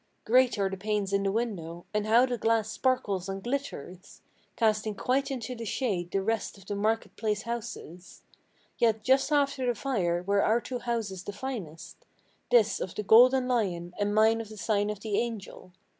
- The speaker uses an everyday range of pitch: Yes, average, 3.5 semitones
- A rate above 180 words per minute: Yes, average, 190 wpm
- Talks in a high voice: Yes, high, 215 Hz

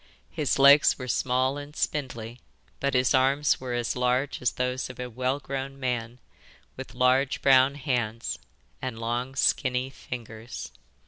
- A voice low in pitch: Yes, low, 130 Hz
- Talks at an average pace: Yes, average, 145 wpm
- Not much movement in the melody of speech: Yes, narrow, 1.7 semitones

